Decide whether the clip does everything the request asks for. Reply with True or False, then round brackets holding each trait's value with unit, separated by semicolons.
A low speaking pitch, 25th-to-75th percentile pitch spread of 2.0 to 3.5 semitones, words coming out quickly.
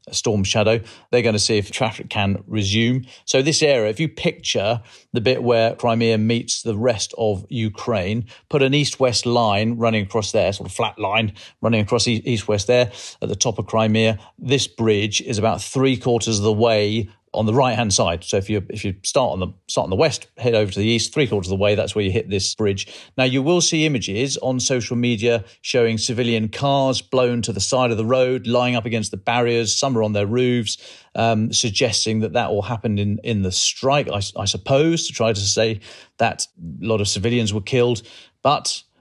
True (115 Hz; 2.6 semitones; 220 wpm)